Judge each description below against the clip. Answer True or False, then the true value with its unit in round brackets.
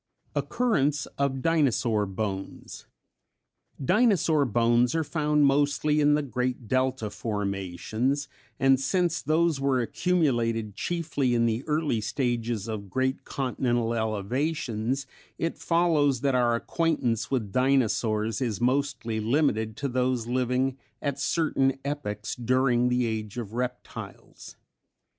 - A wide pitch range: False (4.0 semitones)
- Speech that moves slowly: True (115 wpm)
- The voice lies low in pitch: True (130 Hz)